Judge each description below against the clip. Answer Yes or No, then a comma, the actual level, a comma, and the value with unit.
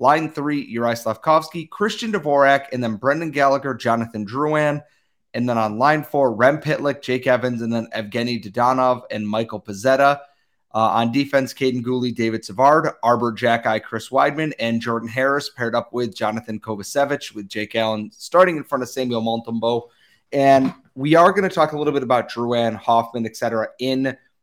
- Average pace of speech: Yes, average, 170 wpm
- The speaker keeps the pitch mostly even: No, average, 3.6 semitones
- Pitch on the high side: No, low, 125 Hz